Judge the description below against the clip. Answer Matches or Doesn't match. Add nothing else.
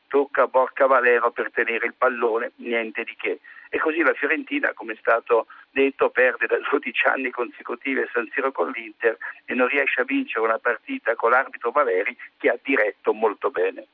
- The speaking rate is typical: Doesn't match